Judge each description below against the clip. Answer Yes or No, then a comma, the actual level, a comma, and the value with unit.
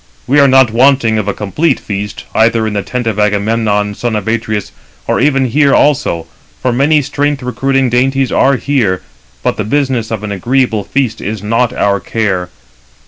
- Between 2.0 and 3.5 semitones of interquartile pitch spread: No, average, 4.4 semitones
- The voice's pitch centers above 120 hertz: No, low, 115 Hz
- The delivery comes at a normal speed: Yes, average, 180 wpm